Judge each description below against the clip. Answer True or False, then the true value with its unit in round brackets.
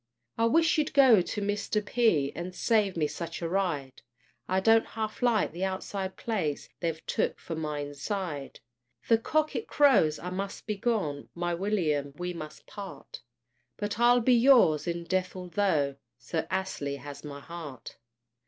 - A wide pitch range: True (5.8 semitones)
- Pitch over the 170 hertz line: True (185 Hz)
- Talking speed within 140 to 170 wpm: True (160 wpm)